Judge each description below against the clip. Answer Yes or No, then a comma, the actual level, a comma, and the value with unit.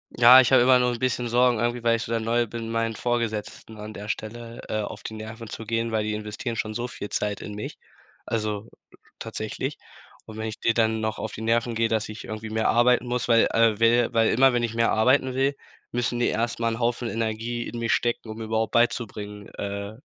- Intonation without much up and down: Yes, narrow, 1.5 semitones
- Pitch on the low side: Yes, low, 115 Hz